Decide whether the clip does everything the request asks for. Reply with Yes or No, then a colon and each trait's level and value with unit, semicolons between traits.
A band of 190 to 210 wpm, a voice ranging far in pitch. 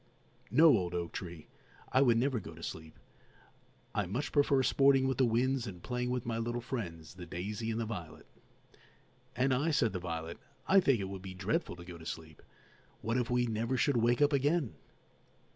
Yes: average, 195 wpm; wide, 6.5 semitones